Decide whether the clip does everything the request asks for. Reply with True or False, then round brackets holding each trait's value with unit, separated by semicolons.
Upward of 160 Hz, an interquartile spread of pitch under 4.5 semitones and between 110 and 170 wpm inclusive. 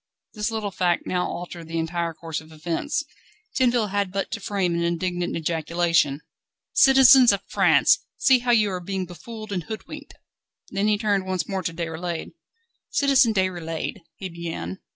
True (185 Hz; 4.0 semitones; 165 wpm)